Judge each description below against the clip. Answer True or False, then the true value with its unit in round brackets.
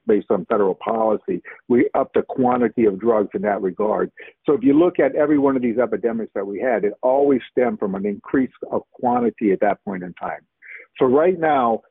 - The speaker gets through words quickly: True (210 wpm)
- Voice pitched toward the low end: True (130 Hz)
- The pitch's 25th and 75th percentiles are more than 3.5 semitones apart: True (4.1 semitones)